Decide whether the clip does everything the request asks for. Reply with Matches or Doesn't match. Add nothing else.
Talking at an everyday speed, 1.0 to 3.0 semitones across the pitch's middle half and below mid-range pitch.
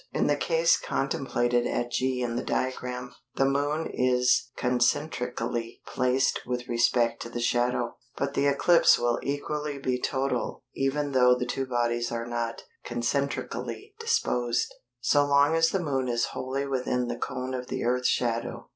Matches